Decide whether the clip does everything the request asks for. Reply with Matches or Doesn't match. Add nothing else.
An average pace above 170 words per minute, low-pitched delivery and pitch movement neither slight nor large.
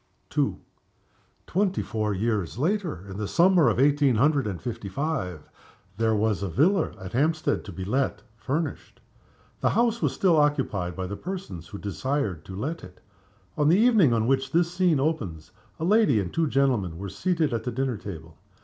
Doesn't match